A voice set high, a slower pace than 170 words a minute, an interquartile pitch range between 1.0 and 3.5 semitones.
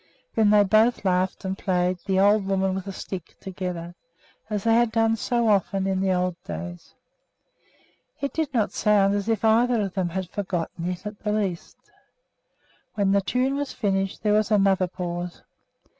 No: high, 195 Hz; average, 175 wpm; narrow, 2.6 semitones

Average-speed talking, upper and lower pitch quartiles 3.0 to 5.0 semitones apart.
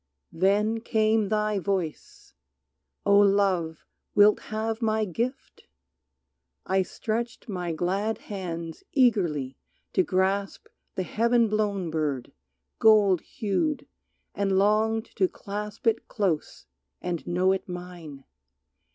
No: slow, 110 wpm; average, 3.4 semitones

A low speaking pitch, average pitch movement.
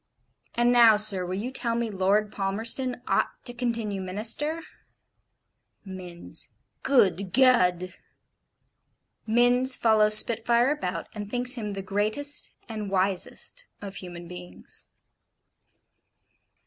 No: high, 215 Hz; average, 4.1 semitones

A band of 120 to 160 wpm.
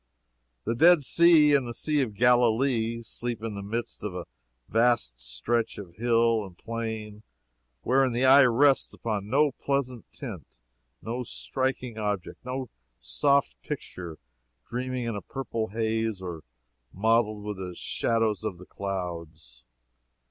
Yes: average, 140 wpm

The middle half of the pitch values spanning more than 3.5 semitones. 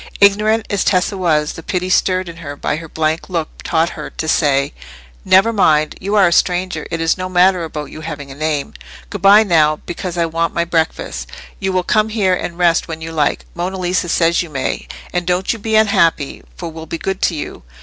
No: average, 2.7 semitones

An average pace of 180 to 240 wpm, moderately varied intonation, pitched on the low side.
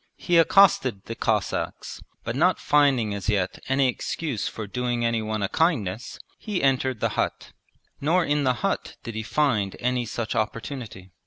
No: average, 160 wpm; average, 4.8 semitones; low, 120 Hz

